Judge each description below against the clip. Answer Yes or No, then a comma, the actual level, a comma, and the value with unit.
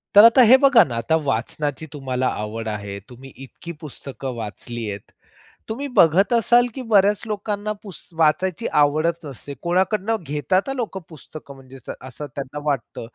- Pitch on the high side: No, medium, 155 Hz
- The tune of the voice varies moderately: No, wide, 7.7 semitones